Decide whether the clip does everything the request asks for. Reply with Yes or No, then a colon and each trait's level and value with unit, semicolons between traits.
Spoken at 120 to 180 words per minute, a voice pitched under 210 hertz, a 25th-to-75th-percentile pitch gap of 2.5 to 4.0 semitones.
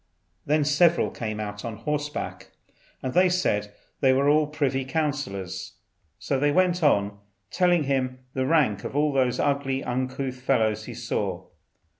Yes: average, 150 wpm; low, 135 Hz; average, 3.3 semitones